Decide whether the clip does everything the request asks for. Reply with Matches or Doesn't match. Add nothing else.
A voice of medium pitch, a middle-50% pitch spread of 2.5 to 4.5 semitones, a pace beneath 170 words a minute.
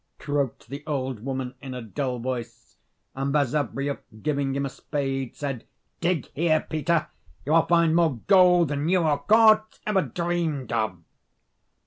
Matches